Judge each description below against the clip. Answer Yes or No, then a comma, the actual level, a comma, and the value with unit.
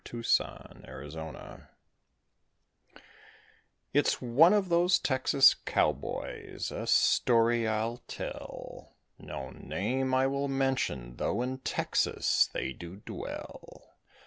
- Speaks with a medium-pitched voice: No, low, 120 Hz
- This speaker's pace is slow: Yes, slow, 100 wpm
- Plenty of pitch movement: Yes, wide, 7.6 semitones